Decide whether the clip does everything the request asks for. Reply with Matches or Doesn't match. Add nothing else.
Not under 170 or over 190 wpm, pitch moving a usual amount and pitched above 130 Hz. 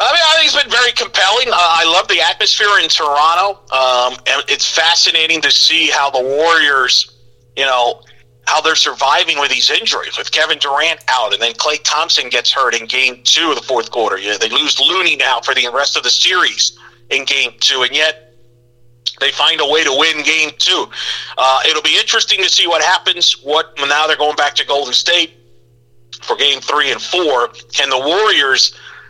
Doesn't match